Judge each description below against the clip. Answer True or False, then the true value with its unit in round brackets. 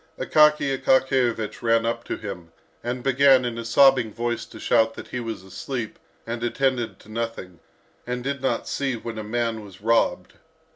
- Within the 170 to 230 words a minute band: True (175 wpm)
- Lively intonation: False (2.6 semitones)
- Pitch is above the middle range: False (115 Hz)